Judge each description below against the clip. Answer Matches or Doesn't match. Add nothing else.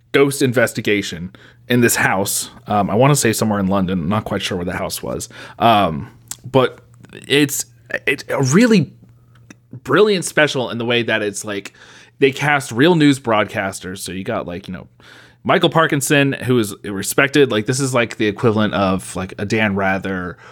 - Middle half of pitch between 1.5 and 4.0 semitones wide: Doesn't match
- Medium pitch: Doesn't match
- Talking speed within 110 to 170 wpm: Doesn't match